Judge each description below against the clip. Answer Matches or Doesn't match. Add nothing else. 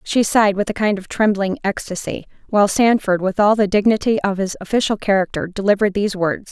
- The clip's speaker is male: Doesn't match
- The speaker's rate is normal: Matches